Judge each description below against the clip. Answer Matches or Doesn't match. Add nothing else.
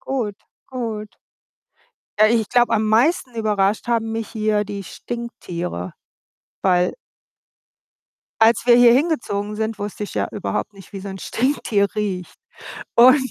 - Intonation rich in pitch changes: Doesn't match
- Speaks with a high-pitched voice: Matches